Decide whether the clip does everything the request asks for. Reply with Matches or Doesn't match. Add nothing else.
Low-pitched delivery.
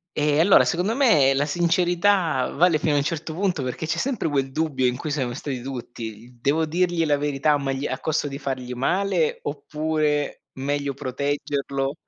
Doesn't match